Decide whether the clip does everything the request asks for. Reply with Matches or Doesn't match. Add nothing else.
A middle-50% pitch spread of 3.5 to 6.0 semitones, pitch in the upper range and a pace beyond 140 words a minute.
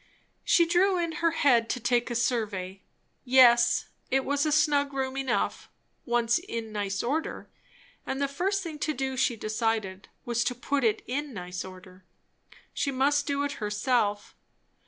Matches